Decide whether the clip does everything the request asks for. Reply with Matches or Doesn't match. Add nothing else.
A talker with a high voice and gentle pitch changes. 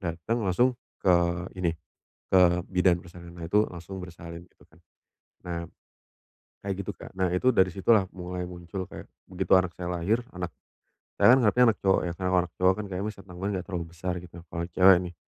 Doesn't match